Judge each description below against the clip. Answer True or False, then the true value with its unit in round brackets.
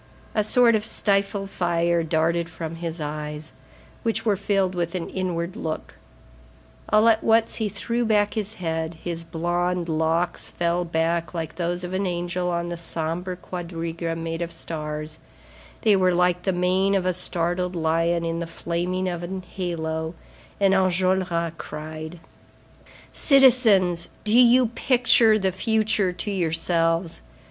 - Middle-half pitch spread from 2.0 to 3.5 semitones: True (2.7 semitones)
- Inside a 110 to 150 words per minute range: True (145 wpm)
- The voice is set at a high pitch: False (175 Hz)